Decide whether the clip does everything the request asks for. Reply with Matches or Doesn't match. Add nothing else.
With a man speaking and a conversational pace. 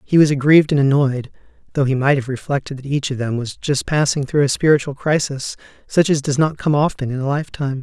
Doesn't match